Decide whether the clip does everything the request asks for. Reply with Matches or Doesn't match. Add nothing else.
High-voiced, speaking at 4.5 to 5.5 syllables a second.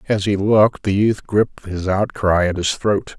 Doesn't match